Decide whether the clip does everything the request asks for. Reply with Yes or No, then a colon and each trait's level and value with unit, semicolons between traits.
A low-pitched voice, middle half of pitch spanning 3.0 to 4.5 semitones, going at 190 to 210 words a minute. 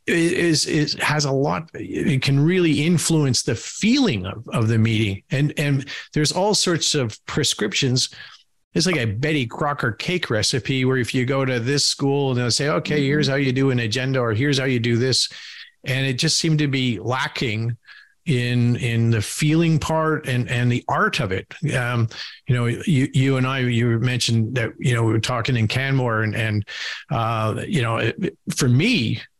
Yes: low, 130 Hz; average, 3.8 semitones; average, 195 wpm